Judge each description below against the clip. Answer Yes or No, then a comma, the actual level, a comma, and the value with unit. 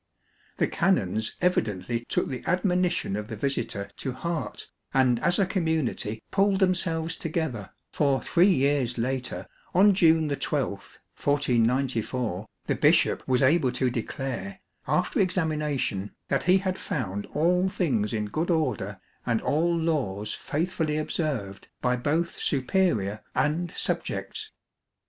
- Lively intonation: Yes, wide, 6.6 semitones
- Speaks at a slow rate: Yes, slow, 130 wpm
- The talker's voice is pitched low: No, medium, 145 Hz